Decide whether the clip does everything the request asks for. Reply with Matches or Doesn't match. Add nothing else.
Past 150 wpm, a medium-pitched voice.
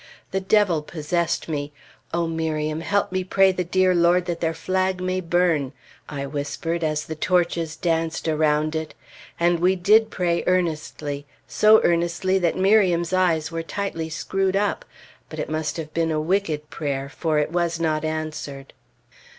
Matches